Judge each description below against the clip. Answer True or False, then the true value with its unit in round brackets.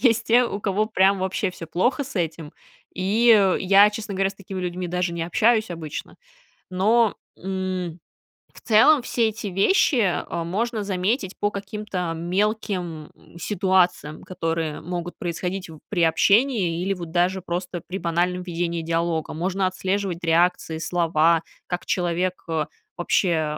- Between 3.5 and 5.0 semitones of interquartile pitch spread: False (2.9 semitones)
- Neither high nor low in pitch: True (180 Hz)